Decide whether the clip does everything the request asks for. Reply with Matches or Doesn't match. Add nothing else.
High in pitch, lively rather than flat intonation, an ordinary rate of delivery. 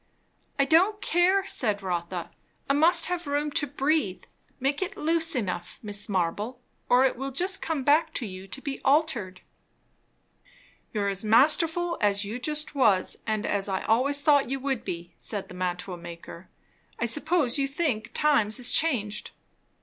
Matches